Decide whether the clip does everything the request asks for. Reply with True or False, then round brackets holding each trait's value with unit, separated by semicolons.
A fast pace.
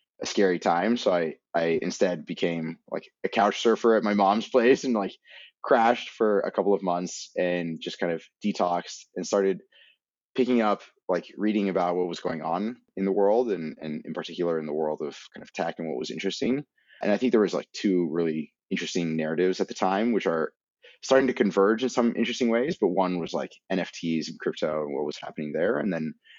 True (215 wpm)